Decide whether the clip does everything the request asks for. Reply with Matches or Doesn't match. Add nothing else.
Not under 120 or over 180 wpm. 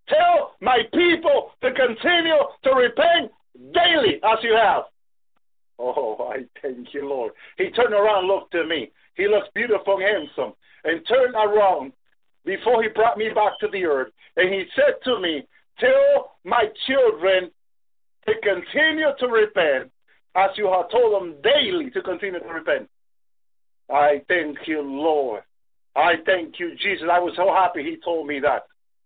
Matches